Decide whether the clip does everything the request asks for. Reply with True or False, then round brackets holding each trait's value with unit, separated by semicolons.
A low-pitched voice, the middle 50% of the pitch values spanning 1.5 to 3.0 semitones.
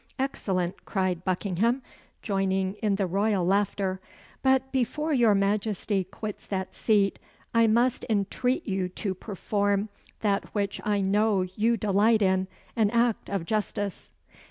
False (205 Hz; 2.6 semitones)